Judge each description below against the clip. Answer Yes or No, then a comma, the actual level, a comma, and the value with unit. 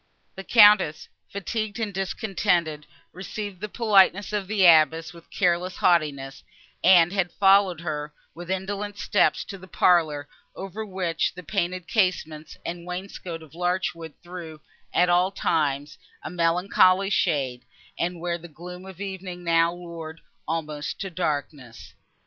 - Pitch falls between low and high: Yes, medium, 175 Hz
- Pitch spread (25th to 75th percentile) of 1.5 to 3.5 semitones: Yes, average, 2.9 semitones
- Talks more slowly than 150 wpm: Yes, average, 140 wpm